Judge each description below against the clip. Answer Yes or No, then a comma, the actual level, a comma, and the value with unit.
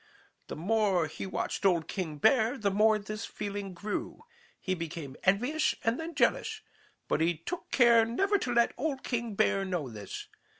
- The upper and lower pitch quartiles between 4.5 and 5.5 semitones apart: Yes, average, 5.1 semitones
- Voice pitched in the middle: No, high, 210 Hz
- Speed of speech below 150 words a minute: No, average, 170 wpm